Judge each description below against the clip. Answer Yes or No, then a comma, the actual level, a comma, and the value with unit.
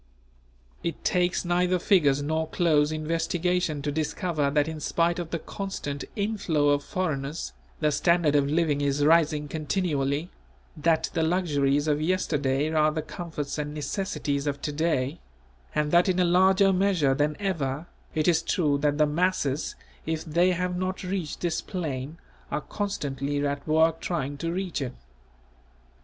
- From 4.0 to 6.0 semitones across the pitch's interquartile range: No, average, 3.4 semitones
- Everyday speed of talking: Yes, average, 155 wpm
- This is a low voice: No, medium, 155 Hz